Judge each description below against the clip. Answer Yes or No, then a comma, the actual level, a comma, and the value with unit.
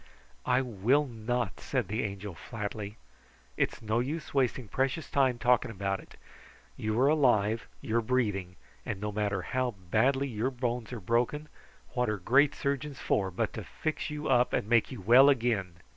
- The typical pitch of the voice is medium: No, low, 120 Hz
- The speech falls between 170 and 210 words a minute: Yes, average, 175 wpm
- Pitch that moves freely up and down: No, average, 3.9 semitones